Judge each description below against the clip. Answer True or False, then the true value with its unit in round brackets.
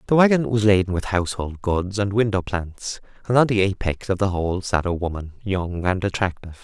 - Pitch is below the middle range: True (95 Hz)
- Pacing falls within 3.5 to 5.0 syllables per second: False (5.6 syllables/s)